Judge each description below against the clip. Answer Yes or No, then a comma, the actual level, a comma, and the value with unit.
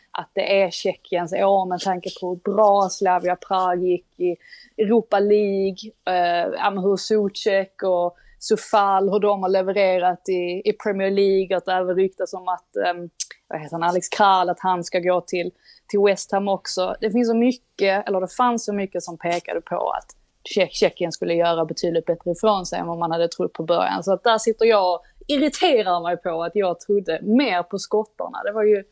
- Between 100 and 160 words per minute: No, fast, 195 wpm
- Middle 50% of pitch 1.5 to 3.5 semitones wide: Yes, narrow, 2.4 semitones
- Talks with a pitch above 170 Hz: Yes, high, 190 Hz